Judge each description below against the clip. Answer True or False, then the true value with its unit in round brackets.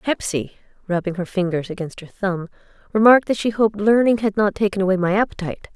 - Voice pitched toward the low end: False (195 Hz)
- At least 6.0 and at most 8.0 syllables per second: True (6.4 syllables/s)